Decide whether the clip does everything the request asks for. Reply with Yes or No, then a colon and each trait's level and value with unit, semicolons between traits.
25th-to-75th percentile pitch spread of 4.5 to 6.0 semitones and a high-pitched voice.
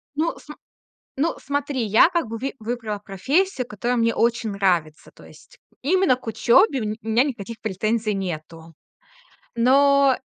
Yes: average, 4.8 semitones; high, 235 Hz